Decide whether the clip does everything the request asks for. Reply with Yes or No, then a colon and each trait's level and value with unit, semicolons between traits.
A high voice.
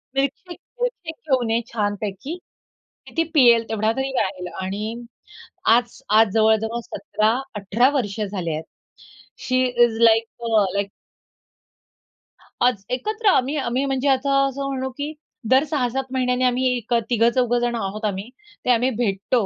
Yes: high, 240 Hz